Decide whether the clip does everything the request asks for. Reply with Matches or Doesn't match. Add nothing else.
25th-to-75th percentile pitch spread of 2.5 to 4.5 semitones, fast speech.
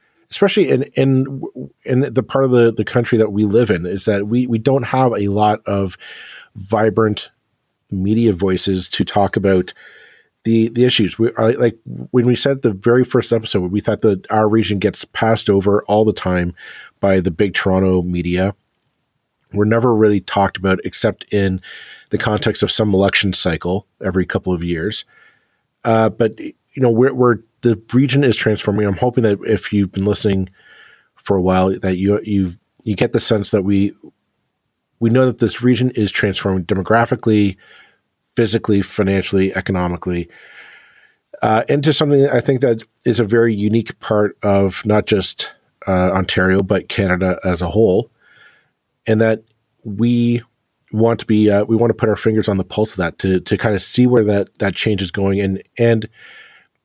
Doesn't match